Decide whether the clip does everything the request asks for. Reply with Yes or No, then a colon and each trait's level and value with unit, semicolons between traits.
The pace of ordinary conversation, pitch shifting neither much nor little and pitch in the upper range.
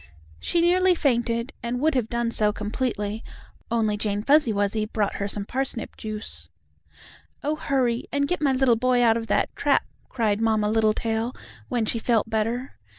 Yes: average, 165 wpm; average, 3.2 semitones; high, 230 Hz